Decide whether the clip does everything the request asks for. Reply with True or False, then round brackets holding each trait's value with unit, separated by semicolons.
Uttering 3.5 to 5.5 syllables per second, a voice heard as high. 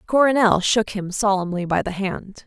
True (4.7 syllables/s; 205 Hz)